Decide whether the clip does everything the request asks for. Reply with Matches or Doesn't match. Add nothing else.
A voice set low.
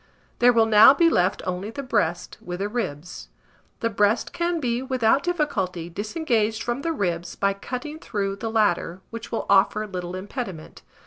Doesn't match